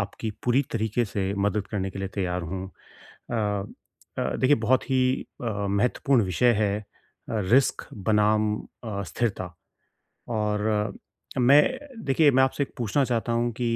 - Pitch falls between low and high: No, low, 110 Hz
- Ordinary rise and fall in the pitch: Yes, average, 3.6 semitones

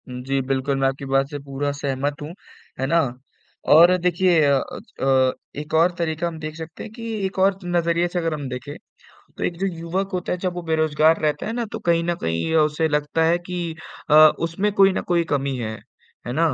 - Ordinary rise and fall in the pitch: Yes, average, 3.7 semitones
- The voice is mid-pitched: Yes, medium, 160 Hz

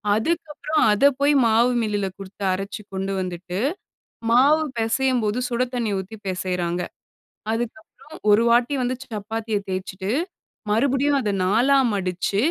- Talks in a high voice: Yes, high, 225 Hz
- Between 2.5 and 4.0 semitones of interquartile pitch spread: No, average, 4.7 semitones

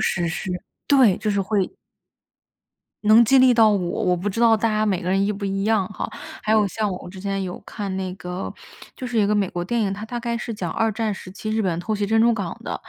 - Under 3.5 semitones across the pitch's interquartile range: Yes, average, 2.7 semitones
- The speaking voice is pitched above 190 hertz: Yes, high, 205 Hz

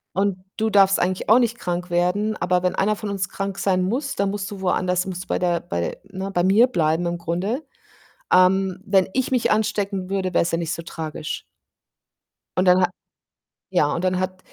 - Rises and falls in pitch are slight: Yes, narrow, 2.1 semitones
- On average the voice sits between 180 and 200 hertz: Yes, medium, 185 Hz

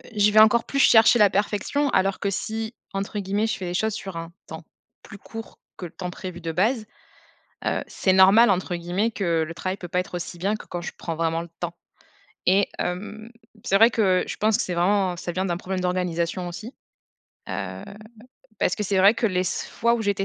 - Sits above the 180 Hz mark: Yes, high, 190 Hz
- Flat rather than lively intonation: No, average, 3.4 semitones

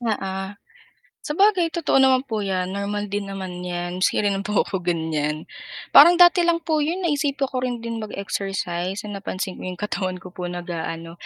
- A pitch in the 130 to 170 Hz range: No, high, 200 Hz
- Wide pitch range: Yes, wide, 6.5 semitones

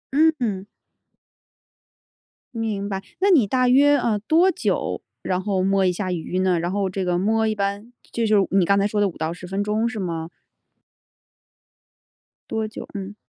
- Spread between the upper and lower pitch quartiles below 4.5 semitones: Yes, average, 3.0 semitones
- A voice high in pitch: Yes, high, 200 Hz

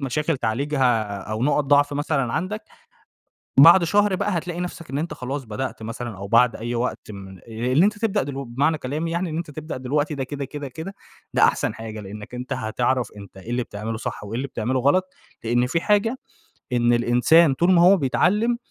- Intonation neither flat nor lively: No, wide, 5.8 semitones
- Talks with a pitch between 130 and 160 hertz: Yes, low, 135 Hz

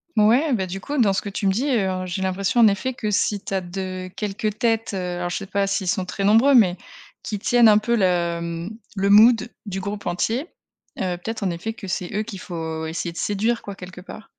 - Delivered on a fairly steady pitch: No, average, 3.1 semitones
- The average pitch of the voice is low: No, high, 195 Hz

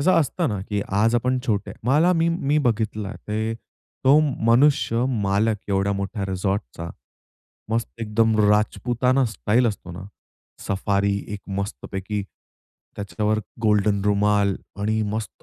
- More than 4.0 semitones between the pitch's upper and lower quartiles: No, narrow, 2.6 semitones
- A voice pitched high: No, low, 105 Hz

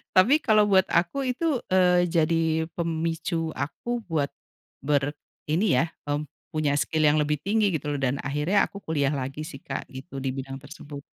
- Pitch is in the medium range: Yes, medium, 155 Hz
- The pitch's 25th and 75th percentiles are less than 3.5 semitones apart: No, average, 3.9 semitones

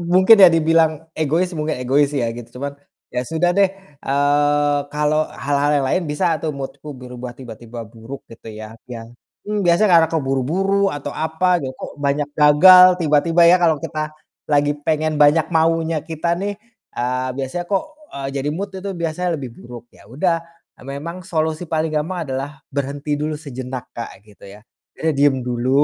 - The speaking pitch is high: No, medium, 150 Hz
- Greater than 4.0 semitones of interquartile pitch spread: No, average, 3.5 semitones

